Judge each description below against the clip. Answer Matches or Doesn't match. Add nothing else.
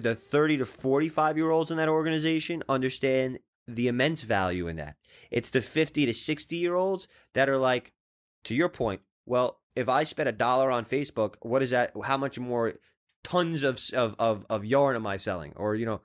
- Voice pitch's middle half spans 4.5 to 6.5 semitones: Matches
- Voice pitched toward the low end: Matches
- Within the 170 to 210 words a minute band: Matches